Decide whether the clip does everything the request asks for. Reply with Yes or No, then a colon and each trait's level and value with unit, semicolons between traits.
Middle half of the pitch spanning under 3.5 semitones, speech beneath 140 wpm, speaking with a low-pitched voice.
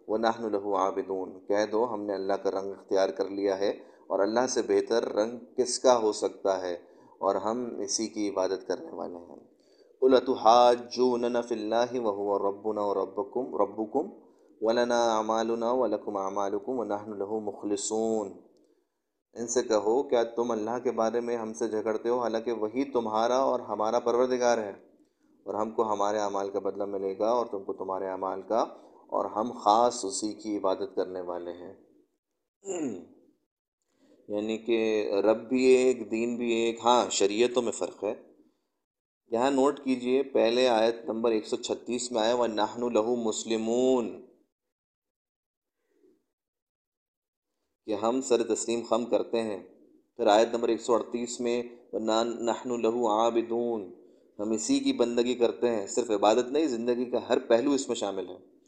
No: narrow, 2.6 semitones; average, 160 wpm; low, 115 Hz